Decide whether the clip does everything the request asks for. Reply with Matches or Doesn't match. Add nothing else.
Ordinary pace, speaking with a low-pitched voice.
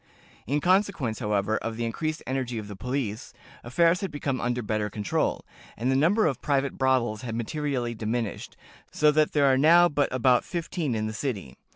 Matches